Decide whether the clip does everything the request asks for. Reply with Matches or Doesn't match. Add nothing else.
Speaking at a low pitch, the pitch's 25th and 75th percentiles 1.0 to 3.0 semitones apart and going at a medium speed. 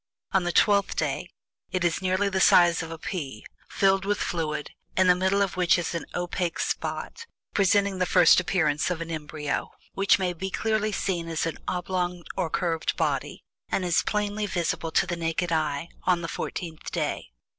Doesn't match